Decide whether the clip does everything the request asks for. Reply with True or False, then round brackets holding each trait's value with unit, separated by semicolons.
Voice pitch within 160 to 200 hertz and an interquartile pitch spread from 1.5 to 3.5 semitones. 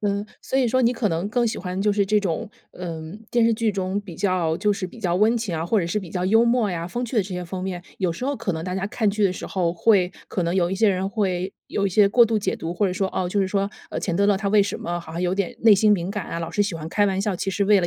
True (195 Hz; 2.8 semitones)